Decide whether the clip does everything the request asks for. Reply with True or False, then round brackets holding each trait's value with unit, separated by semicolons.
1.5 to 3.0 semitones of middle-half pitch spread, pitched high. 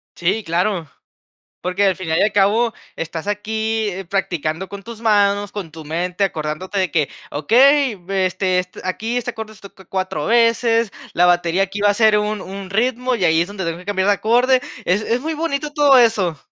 False (3.7 semitones; 200 Hz)